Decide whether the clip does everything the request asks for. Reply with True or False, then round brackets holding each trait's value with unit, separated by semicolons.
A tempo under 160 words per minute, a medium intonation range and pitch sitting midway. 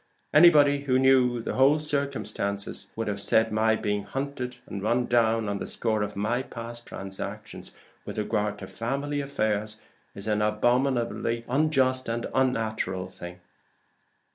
False (145 wpm; 4.0 semitones; 115 Hz)